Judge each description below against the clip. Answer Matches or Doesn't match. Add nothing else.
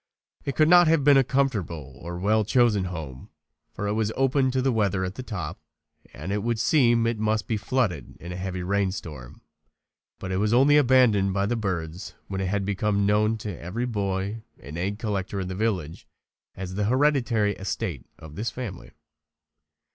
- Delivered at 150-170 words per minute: Doesn't match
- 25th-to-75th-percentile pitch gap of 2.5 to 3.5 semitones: Doesn't match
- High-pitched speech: Doesn't match